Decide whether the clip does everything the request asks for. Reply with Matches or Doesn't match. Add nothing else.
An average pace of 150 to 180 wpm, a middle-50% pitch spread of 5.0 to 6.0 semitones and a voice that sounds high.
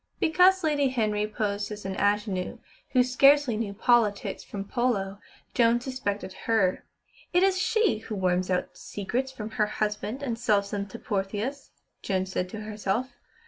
Doesn't match